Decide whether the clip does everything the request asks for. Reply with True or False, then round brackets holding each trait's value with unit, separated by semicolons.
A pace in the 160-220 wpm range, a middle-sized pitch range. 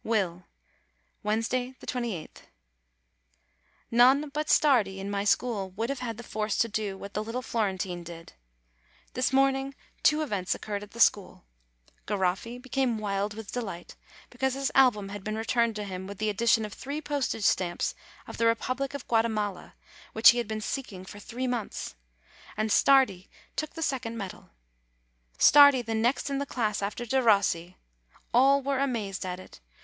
True (165 wpm; 4.3 semitones)